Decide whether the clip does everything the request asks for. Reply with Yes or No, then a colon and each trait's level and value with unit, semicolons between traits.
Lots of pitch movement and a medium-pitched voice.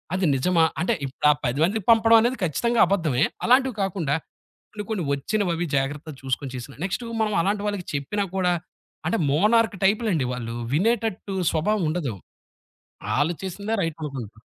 Yes: wide, 6.7 semitones; medium, 180 Hz